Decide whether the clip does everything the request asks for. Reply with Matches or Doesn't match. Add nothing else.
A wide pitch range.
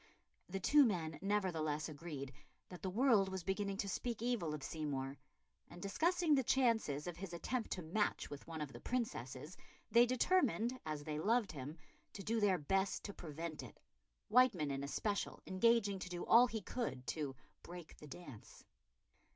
Matches